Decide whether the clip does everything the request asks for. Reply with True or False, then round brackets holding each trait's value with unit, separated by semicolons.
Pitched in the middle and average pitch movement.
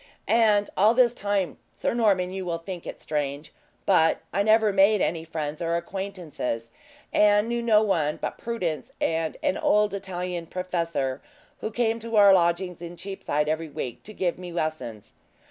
True (180 Hz; 4.2 semitones)